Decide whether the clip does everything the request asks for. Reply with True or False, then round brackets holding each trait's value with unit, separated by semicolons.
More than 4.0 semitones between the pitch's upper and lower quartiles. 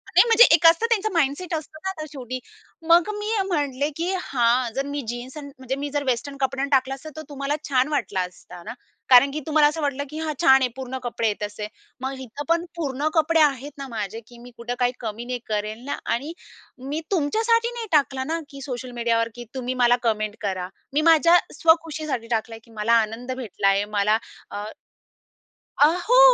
True (4.5 semitones)